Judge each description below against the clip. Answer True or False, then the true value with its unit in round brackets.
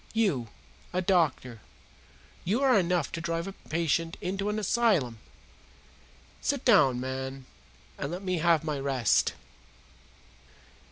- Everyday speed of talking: False (120 wpm)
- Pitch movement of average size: False (6.3 semitones)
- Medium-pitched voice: True (170 Hz)